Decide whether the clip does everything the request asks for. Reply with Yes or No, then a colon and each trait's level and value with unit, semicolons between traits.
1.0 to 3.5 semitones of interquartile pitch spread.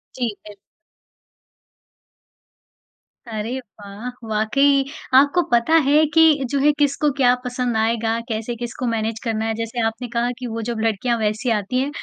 Yes: average, 2.9 semitones